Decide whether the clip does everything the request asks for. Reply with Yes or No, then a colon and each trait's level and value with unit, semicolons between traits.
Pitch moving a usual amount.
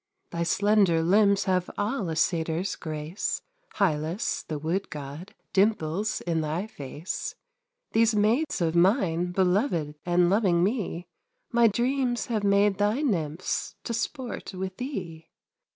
Yes: average, 4.5 semitones